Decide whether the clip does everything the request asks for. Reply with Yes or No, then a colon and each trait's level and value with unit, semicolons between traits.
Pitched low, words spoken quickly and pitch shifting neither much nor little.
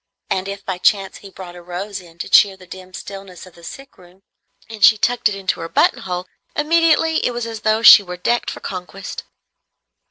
No: high, 195 Hz; fast, 210 wpm; average, 3.2 semitones